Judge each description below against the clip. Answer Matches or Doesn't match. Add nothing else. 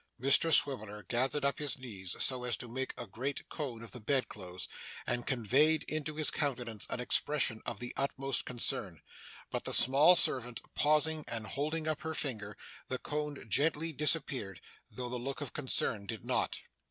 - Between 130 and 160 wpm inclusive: Doesn't match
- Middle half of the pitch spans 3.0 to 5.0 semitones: Matches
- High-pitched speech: Doesn't match